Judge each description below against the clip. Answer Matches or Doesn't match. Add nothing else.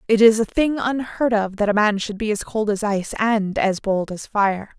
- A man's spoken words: Doesn't match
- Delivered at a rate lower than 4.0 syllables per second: Doesn't match